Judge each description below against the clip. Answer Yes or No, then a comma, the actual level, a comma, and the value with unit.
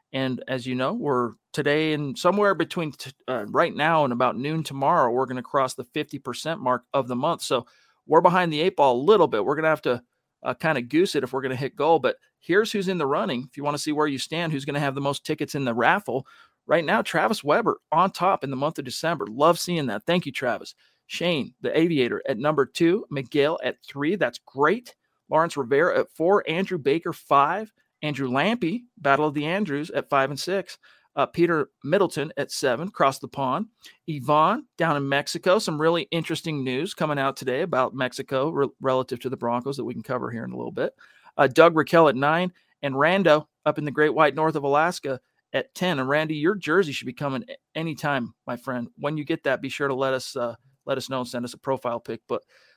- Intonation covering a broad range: No, average, 3.6 semitones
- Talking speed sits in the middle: No, fast, 230 wpm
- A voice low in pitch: No, medium, 145 Hz